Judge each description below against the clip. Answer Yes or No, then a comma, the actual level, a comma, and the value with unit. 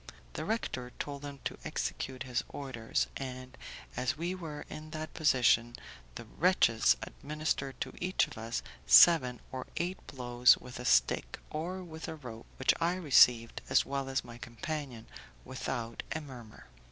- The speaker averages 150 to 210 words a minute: Yes, average, 155 wpm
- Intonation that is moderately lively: Yes, average, 4.3 semitones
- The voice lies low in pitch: Yes, low, 130 Hz